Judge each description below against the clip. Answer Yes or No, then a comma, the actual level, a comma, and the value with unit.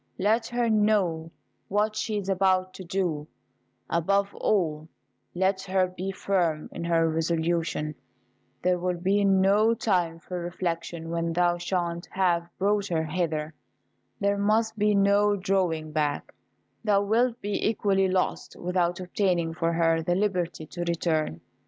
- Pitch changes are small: No, average, 3.1 semitones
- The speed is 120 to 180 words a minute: Yes, average, 140 wpm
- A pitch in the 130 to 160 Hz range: No, medium, 180 Hz